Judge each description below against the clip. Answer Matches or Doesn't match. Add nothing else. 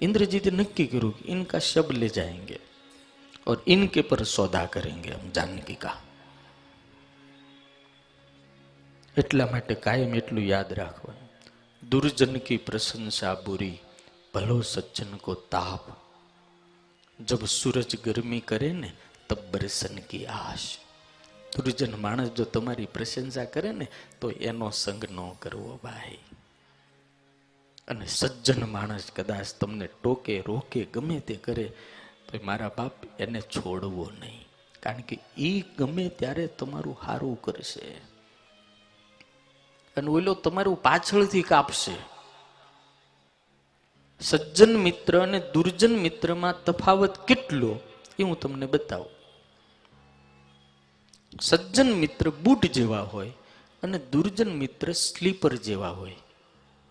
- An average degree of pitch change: Doesn't match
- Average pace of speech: Doesn't match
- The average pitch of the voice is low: Matches